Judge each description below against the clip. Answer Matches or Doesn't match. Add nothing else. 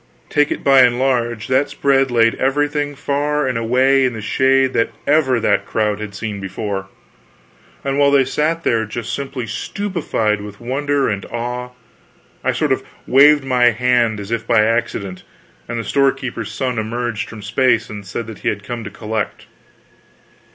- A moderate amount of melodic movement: Matches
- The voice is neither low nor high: Doesn't match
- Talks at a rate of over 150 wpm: Matches